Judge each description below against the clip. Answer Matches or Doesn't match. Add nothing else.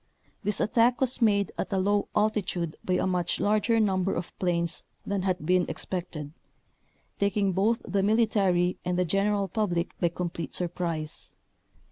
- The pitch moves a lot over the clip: Doesn't match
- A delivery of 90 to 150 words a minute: Doesn't match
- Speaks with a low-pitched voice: Doesn't match